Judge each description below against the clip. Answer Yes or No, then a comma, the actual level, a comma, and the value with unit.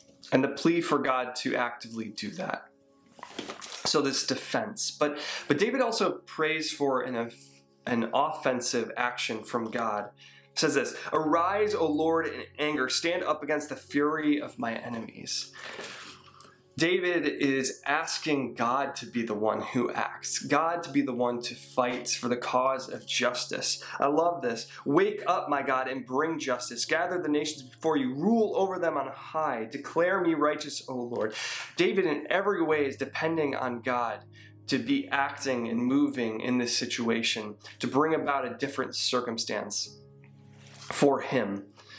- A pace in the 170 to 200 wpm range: No, average, 160 wpm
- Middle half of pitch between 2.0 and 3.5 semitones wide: No, average, 4.2 semitones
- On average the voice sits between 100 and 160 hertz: Yes, low, 135 Hz